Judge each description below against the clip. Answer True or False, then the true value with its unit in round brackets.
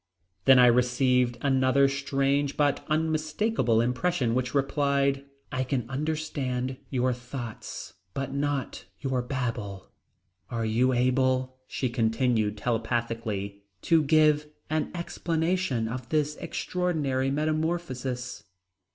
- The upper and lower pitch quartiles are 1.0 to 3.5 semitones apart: True (3.0 semitones)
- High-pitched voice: False (130 Hz)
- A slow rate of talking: True (105 wpm)